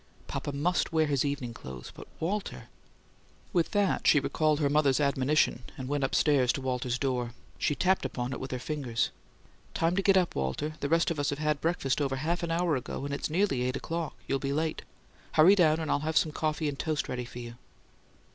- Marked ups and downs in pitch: No, average, 3.6 semitones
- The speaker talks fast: Yes, fast, 215 wpm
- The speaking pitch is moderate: Yes, medium, 145 Hz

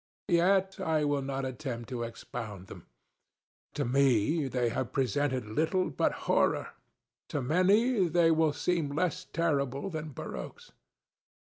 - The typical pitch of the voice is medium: Yes, medium, 145 Hz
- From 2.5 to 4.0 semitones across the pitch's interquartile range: No, average, 4.9 semitones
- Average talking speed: No, slow, 125 wpm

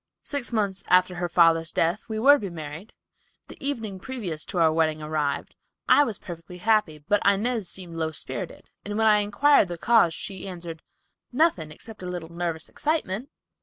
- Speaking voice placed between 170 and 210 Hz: Yes, medium, 185 Hz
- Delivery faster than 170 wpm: Yes, average, 180 wpm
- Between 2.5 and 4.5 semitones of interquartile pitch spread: No, average, 4.9 semitones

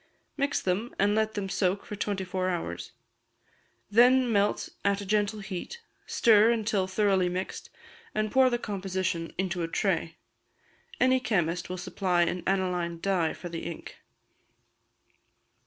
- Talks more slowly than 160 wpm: Yes, average, 140 wpm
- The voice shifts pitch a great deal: No, average, 3.0 semitones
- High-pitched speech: Yes, high, 195 Hz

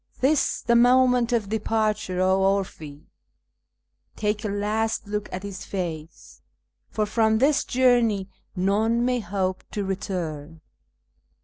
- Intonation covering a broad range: No, average, 3.5 semitones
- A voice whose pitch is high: Yes, high, 210 Hz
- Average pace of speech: No, slow, 125 wpm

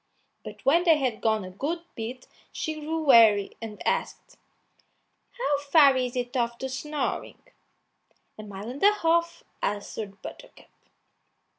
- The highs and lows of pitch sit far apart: Yes, wide, 6.0 semitones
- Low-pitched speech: No, very high, 260 Hz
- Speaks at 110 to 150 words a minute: Yes, average, 140 wpm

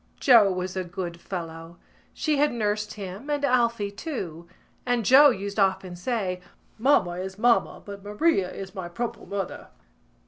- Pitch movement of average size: Yes, average, 4.7 semitones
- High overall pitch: Yes, high, 200 Hz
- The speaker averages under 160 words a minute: Yes, average, 150 wpm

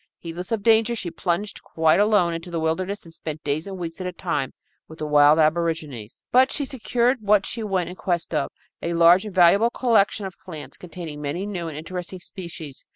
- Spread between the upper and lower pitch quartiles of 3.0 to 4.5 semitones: Yes, average, 3.8 semitones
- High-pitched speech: No, medium, 175 Hz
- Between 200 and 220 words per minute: Yes, fast, 205 wpm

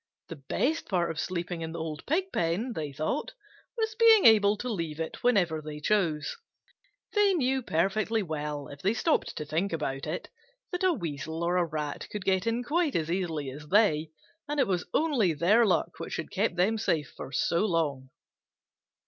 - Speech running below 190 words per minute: Yes, average, 180 wpm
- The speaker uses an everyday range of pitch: No, wide, 6.5 semitones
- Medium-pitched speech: Yes, medium, 175 Hz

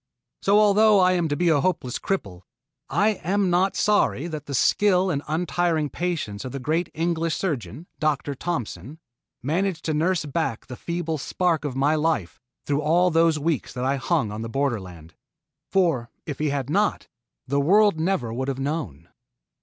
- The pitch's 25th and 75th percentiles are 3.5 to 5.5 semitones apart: Yes, average, 4.7 semitones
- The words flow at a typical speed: Yes, average, 175 wpm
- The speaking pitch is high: No, medium, 155 Hz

